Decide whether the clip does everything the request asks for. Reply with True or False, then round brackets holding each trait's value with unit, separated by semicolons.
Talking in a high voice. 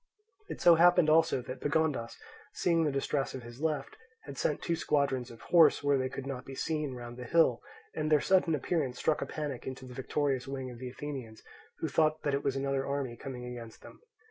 False (140 Hz)